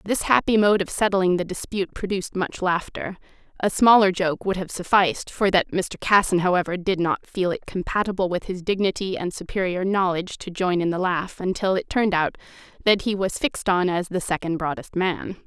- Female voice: Yes, female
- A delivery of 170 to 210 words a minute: Yes, average, 195 wpm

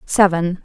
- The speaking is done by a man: No, female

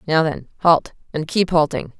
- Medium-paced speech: Yes, average, 150 wpm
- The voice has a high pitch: No, medium, 160 Hz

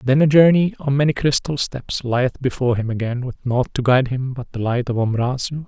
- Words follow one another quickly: Yes, fast, 220 wpm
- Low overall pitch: Yes, low, 130 Hz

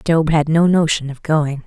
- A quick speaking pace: Yes, fast, 250 wpm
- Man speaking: No, female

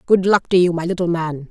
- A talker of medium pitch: Yes, medium, 175 Hz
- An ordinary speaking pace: No, fast, 280 wpm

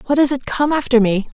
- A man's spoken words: No, female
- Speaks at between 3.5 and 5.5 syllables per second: No, 6.0 syllables/s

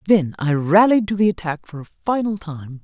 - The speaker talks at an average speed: No, fast, 210 wpm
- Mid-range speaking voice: Yes, medium, 180 Hz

